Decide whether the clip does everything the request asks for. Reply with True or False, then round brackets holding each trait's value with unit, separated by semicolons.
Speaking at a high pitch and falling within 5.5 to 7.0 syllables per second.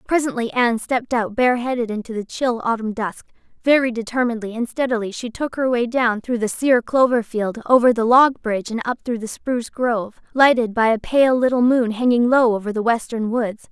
True (235 Hz; 5.6 syllables/s)